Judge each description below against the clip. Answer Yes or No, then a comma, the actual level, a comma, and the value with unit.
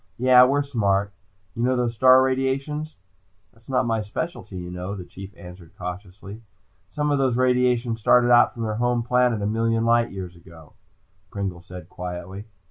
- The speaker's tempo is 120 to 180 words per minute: Yes, average, 170 wpm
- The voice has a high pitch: No, low, 115 Hz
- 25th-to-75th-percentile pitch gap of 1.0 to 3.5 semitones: No, average, 4.7 semitones